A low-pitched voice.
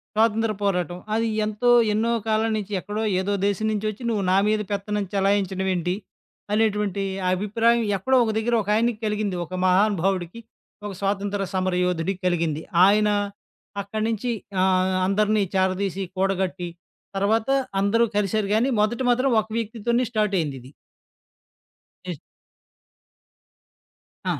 No: high, 205 Hz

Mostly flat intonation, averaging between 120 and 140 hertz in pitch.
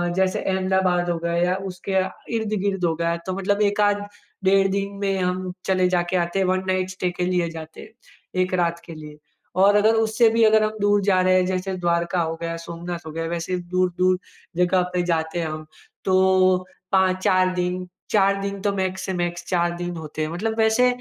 No: narrow, 2.1 semitones; medium, 185 Hz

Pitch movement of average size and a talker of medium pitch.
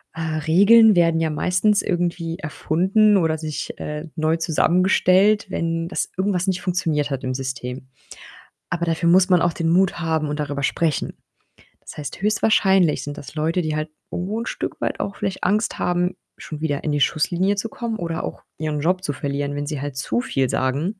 Yes: average, 3.8 semitones; medium, 165 Hz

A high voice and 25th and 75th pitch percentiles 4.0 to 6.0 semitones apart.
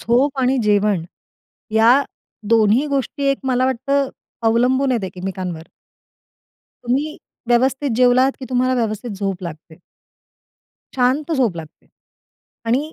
Yes: high, 245 Hz; average, 4.3 semitones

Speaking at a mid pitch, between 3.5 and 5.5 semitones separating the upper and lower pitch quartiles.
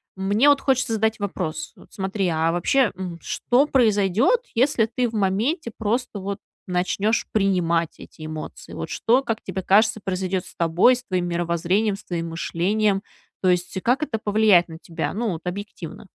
No: high, 200 Hz; average, 4.1 semitones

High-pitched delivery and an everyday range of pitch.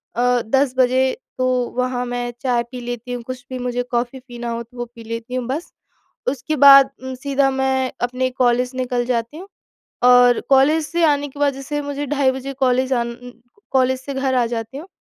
No: very high, 255 Hz; narrow, 1.8 semitones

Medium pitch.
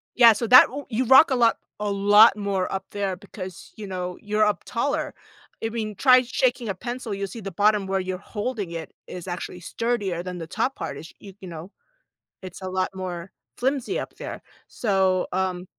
No: high, 200 Hz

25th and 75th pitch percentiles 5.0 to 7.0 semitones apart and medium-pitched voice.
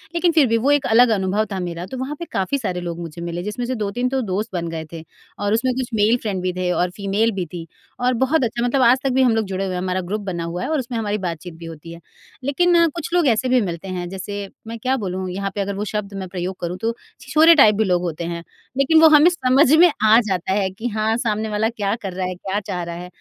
No: wide, 5.4 semitones; high, 205 Hz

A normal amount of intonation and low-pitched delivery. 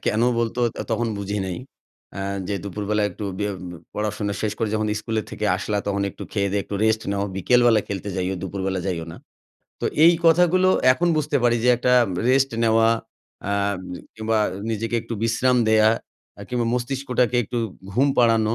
Yes: average, 3.2 semitones; low, 110 Hz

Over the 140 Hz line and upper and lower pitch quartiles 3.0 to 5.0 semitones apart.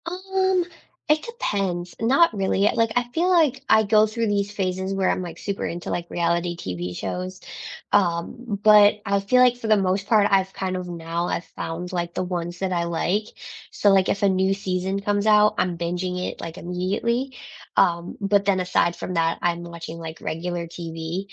Yes: high, 190 Hz; average, 3.4 semitones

